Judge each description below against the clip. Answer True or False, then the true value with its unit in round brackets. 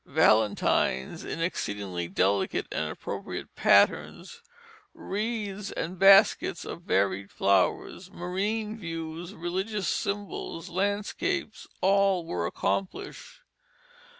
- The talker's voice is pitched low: False (180 Hz)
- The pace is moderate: False (90 wpm)